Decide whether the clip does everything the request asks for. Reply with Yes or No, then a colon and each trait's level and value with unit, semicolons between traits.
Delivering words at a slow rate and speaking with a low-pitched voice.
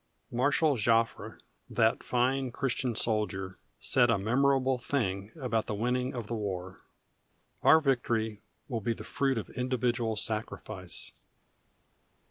Yes: slow, 120 wpm; low, 115 Hz